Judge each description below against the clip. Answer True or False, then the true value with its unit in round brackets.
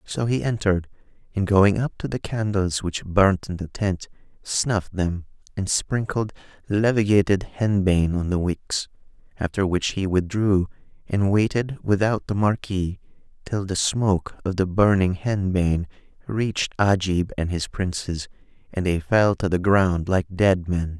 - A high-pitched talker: False (95 Hz)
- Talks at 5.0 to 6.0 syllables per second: False (4.4 syllables/s)